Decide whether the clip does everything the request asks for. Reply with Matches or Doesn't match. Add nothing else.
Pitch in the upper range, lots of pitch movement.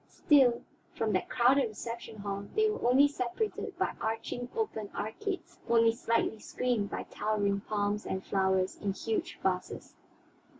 Doesn't match